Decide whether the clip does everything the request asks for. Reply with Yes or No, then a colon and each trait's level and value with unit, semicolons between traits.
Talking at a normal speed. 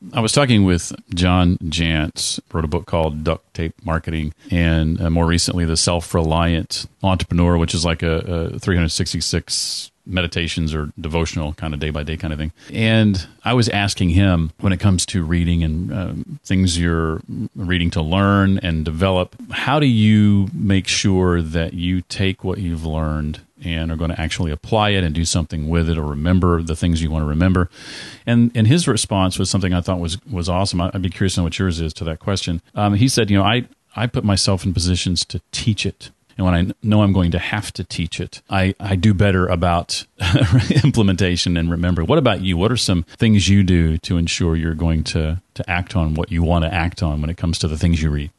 No: fast, 215 wpm